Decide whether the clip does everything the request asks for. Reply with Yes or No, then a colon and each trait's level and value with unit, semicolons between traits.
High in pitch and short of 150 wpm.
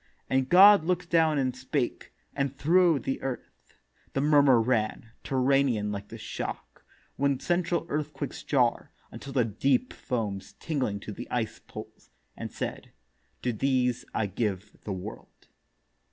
No: low, 130 Hz; average, 140 wpm